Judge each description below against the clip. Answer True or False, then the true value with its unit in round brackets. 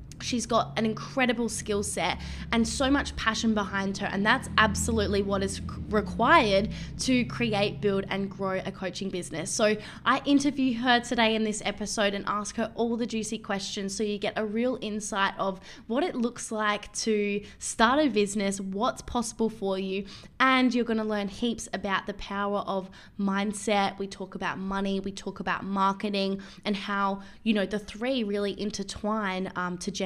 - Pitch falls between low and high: False (205 Hz)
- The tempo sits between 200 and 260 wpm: False (180 wpm)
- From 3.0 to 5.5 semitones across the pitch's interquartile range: False (2.5 semitones)